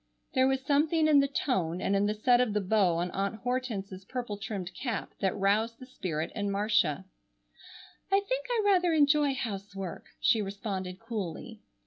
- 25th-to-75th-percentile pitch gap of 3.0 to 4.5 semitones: No, average, 5.3 semitones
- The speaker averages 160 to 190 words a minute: Yes, average, 170 wpm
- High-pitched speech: Yes, high, 215 Hz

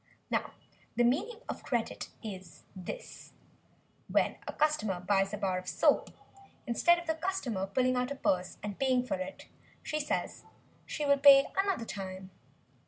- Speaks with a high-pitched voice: Yes, very high, 250 Hz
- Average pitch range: No, wide, 7.3 semitones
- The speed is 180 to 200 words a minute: No, average, 160 wpm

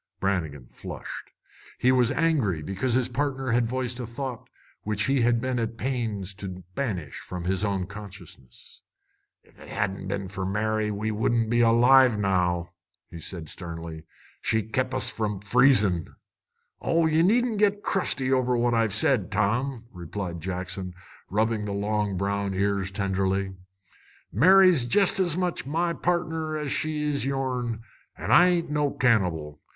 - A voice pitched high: No, low, 110 Hz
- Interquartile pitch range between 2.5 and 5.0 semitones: No, wide, 5.5 semitones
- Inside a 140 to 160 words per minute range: Yes, average, 155 wpm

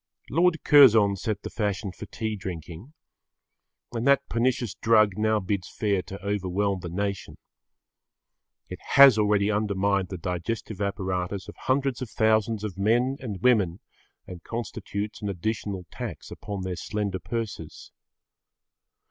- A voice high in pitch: No, low, 105 Hz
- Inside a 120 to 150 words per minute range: Yes, slow, 135 wpm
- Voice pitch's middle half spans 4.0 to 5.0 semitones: No, average, 3.2 semitones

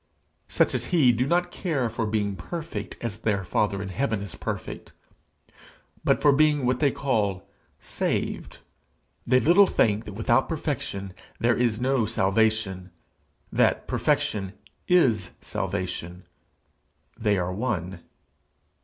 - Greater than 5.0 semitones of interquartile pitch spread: Yes, wide, 5.4 semitones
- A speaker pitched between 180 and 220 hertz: No, low, 110 Hz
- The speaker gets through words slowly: Yes, slow, 125 wpm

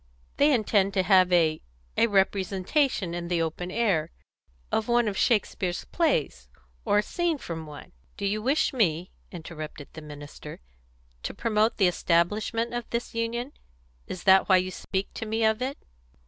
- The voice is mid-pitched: No, high, 195 Hz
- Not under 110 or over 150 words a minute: No, average, 160 wpm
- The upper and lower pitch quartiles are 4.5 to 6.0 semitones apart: Yes, average, 5.0 semitones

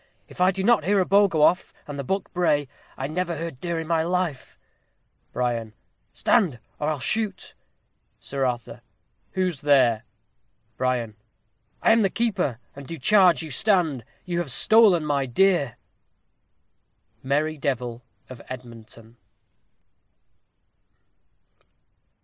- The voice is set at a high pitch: No, medium, 155 Hz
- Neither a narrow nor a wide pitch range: No, wide, 6.1 semitones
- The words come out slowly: Yes, slow, 130 wpm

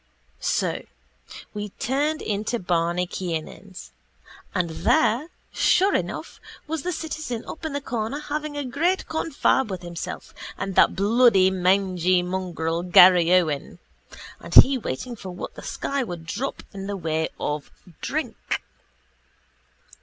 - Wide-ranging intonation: Yes, wide, 7.6 semitones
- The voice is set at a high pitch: Yes, high, 200 Hz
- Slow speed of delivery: Yes, slow, 130 wpm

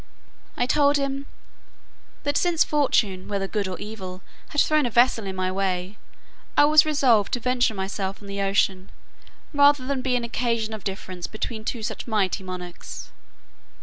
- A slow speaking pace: No, average, 165 wpm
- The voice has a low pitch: No, high, 220 Hz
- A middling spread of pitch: No, wide, 5.8 semitones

